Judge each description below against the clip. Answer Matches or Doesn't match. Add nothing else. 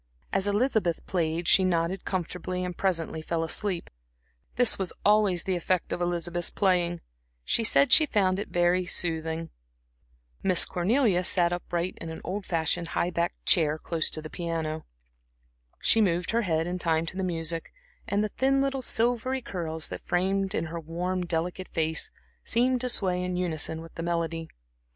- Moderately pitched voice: Matches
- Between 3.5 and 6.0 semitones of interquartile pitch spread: Doesn't match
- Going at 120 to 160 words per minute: Doesn't match